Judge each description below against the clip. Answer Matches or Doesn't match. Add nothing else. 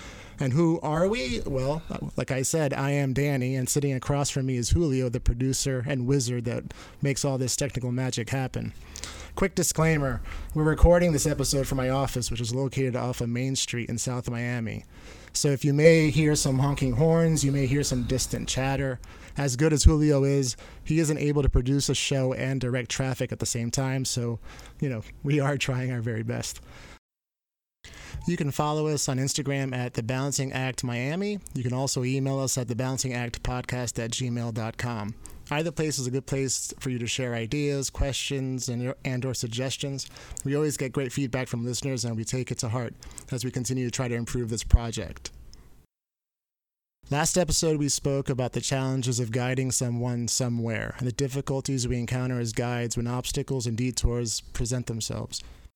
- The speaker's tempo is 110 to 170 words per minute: Doesn't match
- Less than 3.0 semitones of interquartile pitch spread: Matches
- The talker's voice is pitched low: Matches